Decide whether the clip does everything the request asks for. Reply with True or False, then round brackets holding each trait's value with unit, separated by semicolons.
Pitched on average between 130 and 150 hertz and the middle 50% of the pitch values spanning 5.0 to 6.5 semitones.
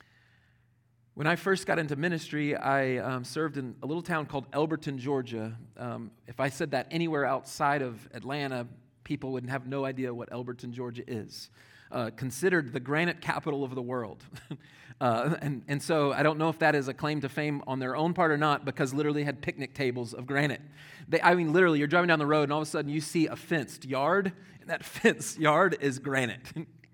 False (140 Hz; 3.5 semitones)